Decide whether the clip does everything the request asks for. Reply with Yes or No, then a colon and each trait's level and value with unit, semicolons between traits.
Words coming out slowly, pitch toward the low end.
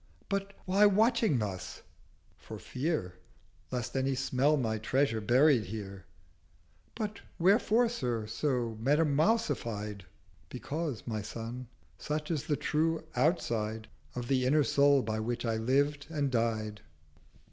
Yes: slow, 120 wpm; low, 130 Hz